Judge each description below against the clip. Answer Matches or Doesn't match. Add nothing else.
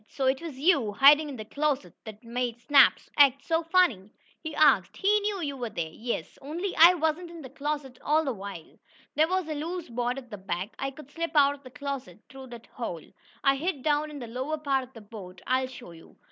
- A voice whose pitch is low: Doesn't match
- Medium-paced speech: Doesn't match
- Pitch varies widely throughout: Doesn't match